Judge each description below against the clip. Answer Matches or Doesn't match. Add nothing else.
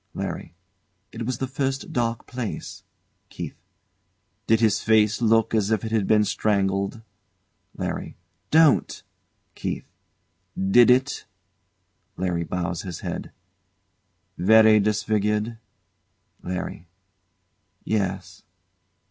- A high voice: Doesn't match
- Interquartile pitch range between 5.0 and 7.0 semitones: Doesn't match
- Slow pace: Matches